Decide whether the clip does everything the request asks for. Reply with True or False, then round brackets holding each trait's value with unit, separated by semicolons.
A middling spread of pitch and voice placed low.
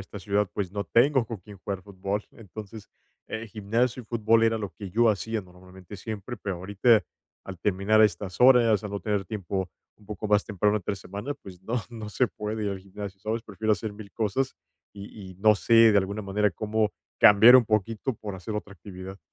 False (2.2 semitones; 105 Hz)